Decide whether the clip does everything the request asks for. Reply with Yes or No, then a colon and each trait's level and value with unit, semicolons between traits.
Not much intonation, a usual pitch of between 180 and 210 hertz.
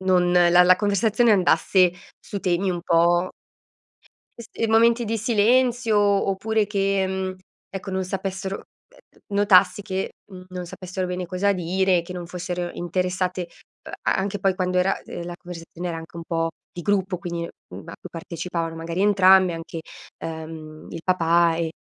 Yes: narrow, 2.3 semitones; medium, 185 Hz